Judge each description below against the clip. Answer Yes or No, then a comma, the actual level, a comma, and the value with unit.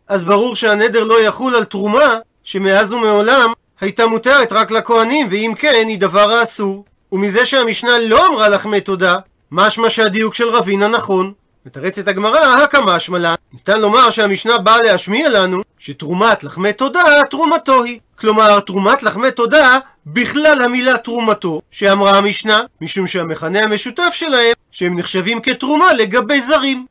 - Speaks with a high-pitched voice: Yes, high, 220 Hz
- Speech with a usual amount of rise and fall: Yes, average, 3.7 semitones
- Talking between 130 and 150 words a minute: Yes, average, 140 wpm